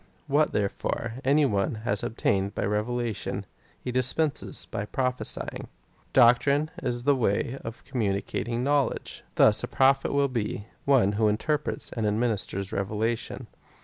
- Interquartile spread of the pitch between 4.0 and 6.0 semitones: Yes, average, 4.5 semitones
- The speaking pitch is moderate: No, low, 120 Hz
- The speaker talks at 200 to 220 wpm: No, average, 140 wpm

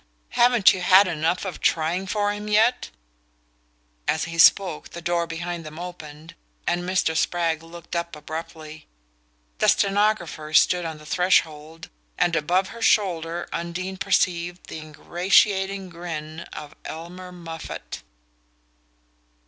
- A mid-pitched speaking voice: Yes, medium, 170 Hz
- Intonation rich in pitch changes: No, narrow, 2.5 semitones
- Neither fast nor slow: No, slow, 125 wpm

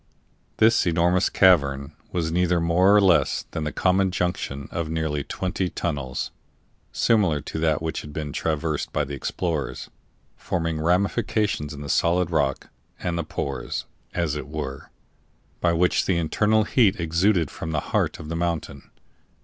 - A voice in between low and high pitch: No, very low, 85 Hz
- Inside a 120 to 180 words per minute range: Yes, average, 155 wpm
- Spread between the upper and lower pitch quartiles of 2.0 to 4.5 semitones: Yes, average, 3.3 semitones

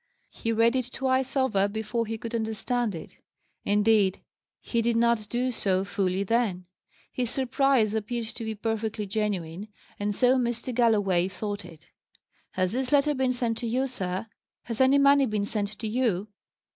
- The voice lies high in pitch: Yes, high, 225 Hz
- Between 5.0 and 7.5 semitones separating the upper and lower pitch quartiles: No, average, 3.4 semitones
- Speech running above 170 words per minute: No, average, 165 wpm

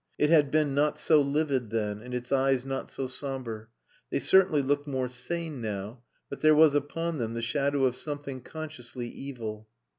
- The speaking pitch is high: No, low, 135 Hz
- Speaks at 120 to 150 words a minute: No, average, 180 wpm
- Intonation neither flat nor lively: Yes, average, 3.4 semitones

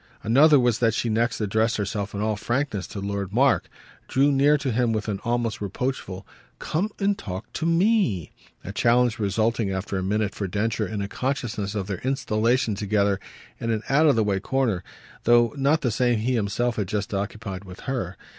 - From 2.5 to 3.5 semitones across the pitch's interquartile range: No, average, 3.9 semitones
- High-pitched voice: No, low, 110 Hz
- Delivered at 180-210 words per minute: Yes, average, 195 wpm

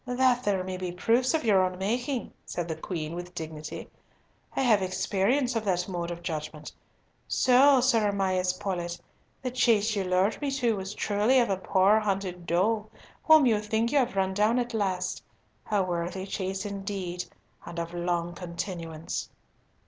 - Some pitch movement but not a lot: Yes, average, 4.2 semitones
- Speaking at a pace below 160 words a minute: No, average, 170 wpm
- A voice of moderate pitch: No, high, 195 Hz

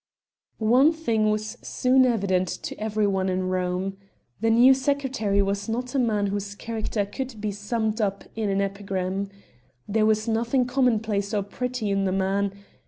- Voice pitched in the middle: No, high, 215 Hz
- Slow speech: No, average, 170 wpm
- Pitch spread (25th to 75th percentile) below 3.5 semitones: Yes, average, 3.1 semitones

